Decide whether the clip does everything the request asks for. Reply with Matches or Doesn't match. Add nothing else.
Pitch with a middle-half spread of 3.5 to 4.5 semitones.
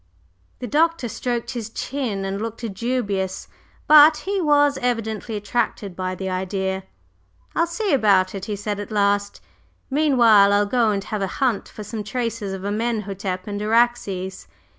Matches